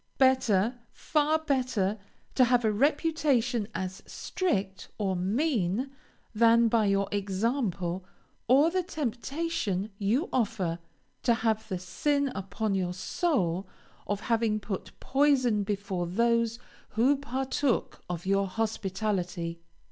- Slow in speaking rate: Yes, slow, 115 wpm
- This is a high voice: Yes, high, 220 Hz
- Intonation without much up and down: No, average, 5.3 semitones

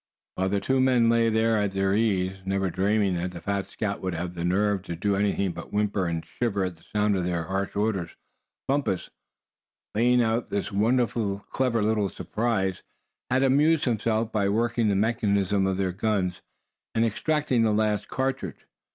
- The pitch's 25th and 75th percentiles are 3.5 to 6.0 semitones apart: No, average, 3.1 semitones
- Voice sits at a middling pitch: No, low, 105 Hz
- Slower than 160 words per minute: No, average, 175 wpm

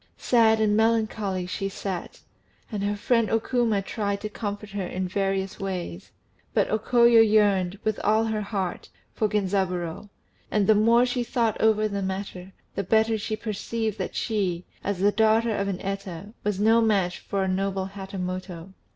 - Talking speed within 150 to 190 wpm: Yes, average, 170 wpm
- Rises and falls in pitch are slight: Yes, narrow, 2.3 semitones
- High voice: Yes, high, 205 Hz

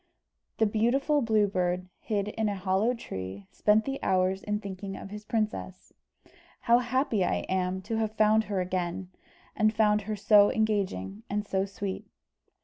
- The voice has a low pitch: No, high, 205 Hz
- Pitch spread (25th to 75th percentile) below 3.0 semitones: Yes, narrow, 2.6 semitones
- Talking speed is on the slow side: No, average, 160 wpm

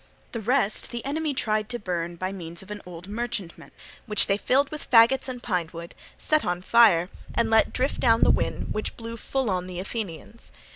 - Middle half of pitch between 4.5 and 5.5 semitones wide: Yes, average, 4.8 semitones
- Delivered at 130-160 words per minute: No, average, 200 wpm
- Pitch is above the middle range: Yes, high, 215 Hz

